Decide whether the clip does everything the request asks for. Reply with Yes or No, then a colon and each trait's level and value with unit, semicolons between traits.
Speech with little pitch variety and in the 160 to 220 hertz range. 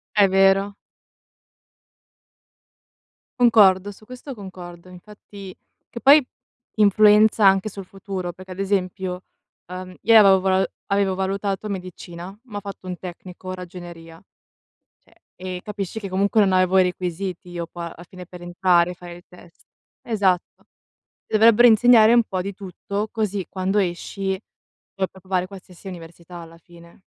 Yes: narrow, 2.0 semitones; high, 190 Hz